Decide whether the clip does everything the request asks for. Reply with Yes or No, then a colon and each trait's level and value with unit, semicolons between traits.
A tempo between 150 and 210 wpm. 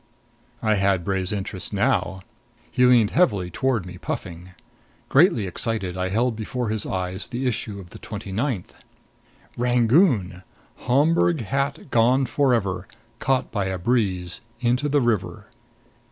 No: slow, 135 wpm